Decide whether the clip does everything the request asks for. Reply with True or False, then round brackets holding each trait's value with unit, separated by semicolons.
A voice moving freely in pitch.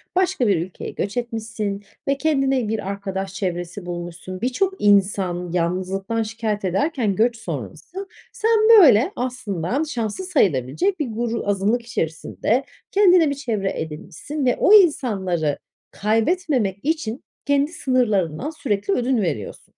True (6.4 semitones)